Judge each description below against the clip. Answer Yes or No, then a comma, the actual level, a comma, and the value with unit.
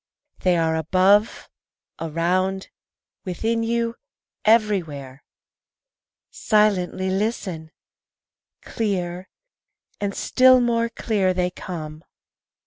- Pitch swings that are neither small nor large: Yes, average, 4.1 semitones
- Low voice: No, high, 190 Hz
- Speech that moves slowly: Yes, slow, 75 wpm